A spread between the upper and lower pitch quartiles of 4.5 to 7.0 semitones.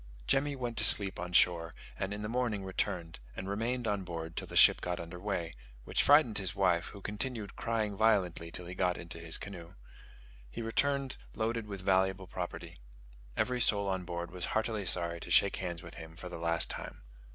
No: average, 4.1 semitones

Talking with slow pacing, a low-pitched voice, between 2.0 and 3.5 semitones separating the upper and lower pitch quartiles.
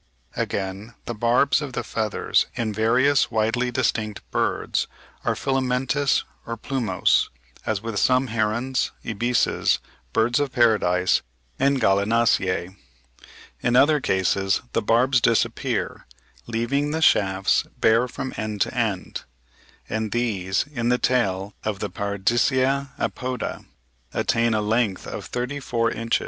Yes: slow, 130 wpm; low, 115 Hz; average, 3.2 semitones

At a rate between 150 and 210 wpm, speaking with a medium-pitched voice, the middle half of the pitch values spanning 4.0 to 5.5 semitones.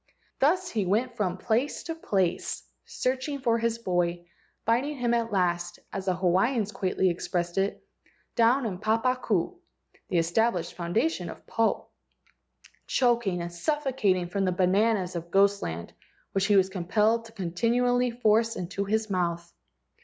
No: average, 155 wpm; high, 205 Hz; average, 4.8 semitones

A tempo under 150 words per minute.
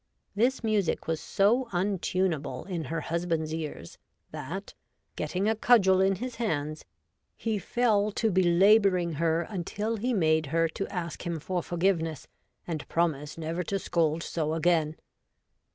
Yes: average, 140 wpm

